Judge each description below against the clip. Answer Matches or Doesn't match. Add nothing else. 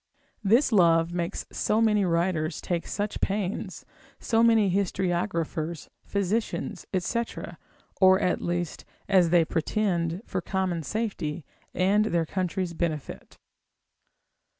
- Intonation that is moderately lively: Matches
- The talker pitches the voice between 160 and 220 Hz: Matches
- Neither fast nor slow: Doesn't match